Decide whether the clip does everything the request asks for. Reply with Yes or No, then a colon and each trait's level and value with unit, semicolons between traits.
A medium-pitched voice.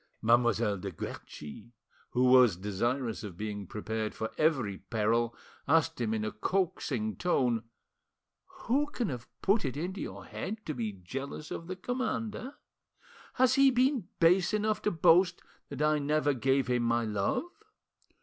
No: low, 130 Hz